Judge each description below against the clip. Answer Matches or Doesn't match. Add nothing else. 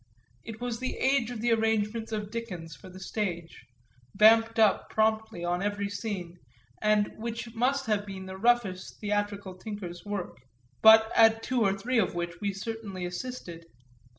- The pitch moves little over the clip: Doesn't match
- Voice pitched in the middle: Doesn't match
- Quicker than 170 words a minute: Doesn't match